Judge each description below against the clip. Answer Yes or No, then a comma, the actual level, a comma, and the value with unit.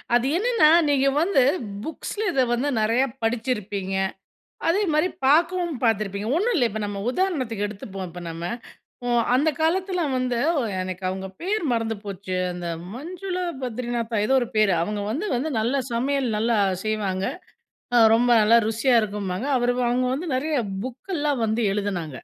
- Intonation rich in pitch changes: Yes, wide, 6.4 semitones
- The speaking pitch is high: Yes, high, 240 Hz